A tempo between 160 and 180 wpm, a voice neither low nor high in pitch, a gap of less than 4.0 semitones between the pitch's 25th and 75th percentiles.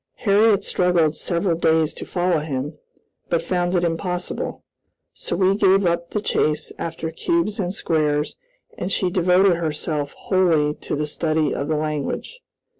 No: average, 150 wpm; medium, 170 Hz; average, 3.2 semitones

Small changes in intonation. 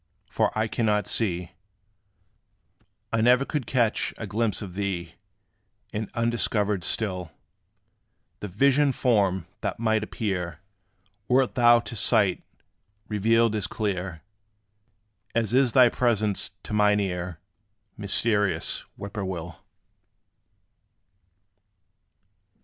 No: average, 3.3 semitones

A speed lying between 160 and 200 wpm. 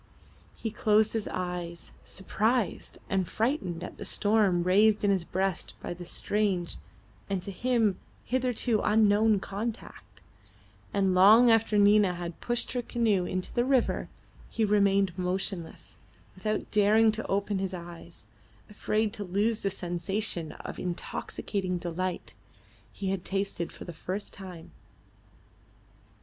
No: slow, 135 wpm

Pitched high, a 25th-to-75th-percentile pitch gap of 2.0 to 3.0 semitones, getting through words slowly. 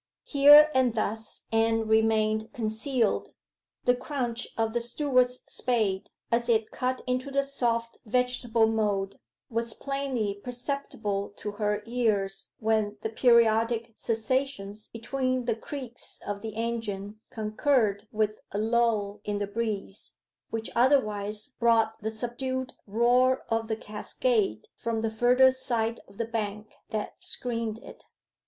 Yes: high, 225 Hz; narrow, 2.6 semitones; slow, 130 wpm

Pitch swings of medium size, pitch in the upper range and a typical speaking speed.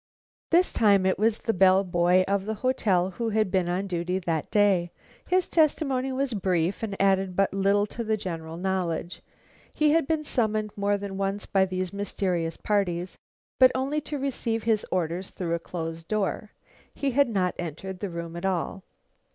Yes: average, 3.7 semitones; high, 195 Hz; average, 180 wpm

